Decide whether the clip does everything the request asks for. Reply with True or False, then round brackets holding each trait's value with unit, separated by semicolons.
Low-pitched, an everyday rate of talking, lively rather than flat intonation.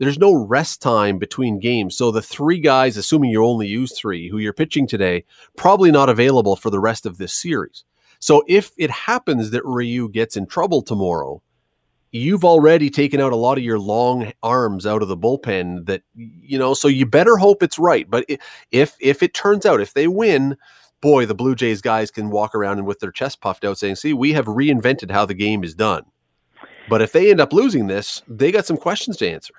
False (125 Hz; 215 wpm; 5.7 semitones)